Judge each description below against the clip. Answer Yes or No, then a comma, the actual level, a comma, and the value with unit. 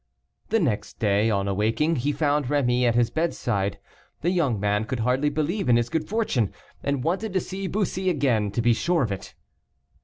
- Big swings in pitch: Yes, wide, 6.6 semitones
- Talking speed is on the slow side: No, average, 190 wpm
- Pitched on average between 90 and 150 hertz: Yes, low, 135 Hz